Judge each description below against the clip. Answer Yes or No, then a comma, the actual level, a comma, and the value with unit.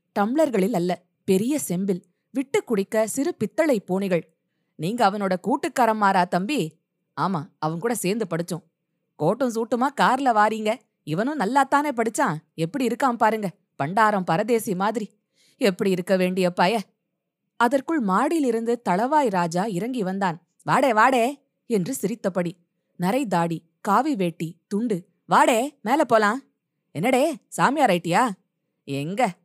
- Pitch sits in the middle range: No, high, 200 Hz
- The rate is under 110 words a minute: No, average, 120 wpm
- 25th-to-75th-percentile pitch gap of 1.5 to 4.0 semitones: No, average, 5.2 semitones